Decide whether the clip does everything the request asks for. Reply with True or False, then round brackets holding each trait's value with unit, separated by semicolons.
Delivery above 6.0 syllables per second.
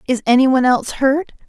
True (6.9 syllables/s)